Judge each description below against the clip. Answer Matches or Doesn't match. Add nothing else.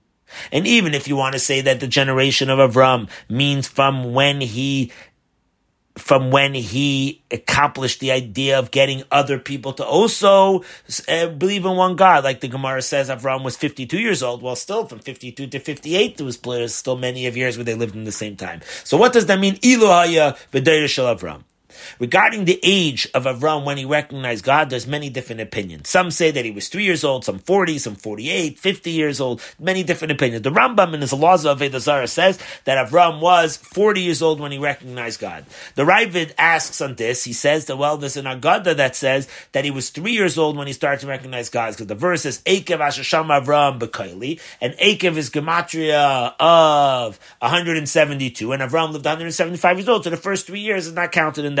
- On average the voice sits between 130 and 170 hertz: Matches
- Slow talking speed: Doesn't match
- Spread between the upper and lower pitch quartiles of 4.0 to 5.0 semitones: Matches